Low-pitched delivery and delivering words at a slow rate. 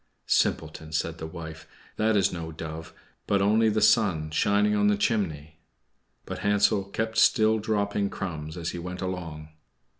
No: very low, 95 Hz; average, 155 wpm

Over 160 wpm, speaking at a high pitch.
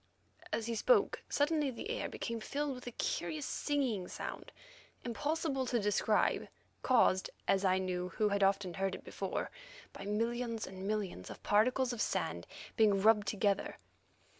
No: average, 155 wpm; high, 215 Hz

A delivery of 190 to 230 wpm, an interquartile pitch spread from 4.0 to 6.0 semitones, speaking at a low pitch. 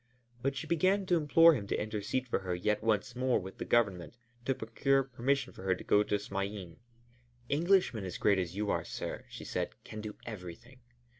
Yes: average, 200 wpm; wide, 5.4 semitones; low, 110 Hz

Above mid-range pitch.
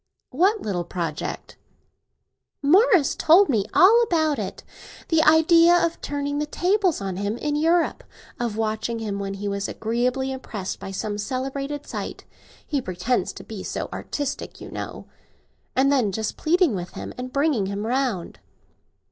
Yes: very high, 265 Hz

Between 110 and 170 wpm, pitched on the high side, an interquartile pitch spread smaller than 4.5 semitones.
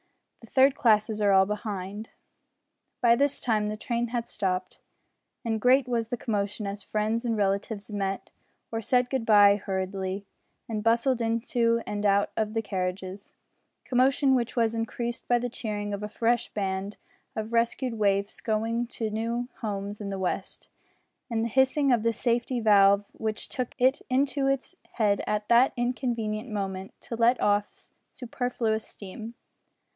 Yes: average, 160 wpm; high, 225 Hz; average, 2.8 semitones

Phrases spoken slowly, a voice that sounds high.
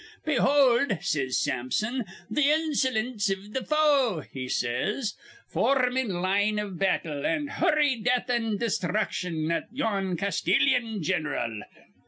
Yes: slow, 130 wpm; high, 215 Hz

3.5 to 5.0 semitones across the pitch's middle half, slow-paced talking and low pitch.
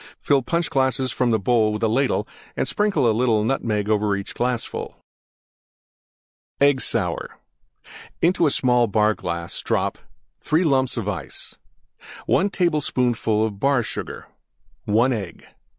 Yes: average, 4.2 semitones; slow, 120 wpm; low, 120 Hz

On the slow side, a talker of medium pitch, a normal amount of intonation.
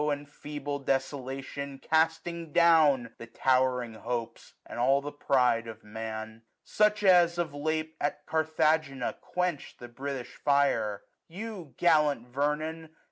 Yes: slow, 130 wpm; medium, 145 Hz; average, 4.1 semitones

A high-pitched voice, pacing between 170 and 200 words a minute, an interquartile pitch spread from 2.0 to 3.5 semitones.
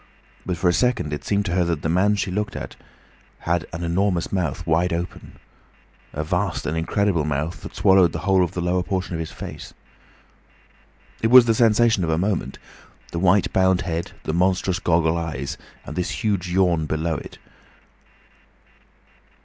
No: very low, 90 Hz; average, 175 wpm; average, 2.8 semitones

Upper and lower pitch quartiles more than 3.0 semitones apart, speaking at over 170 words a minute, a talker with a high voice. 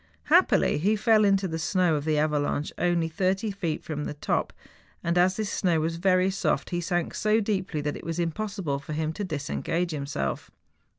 No: average, 3.8 semitones; average, 190 wpm; medium, 170 Hz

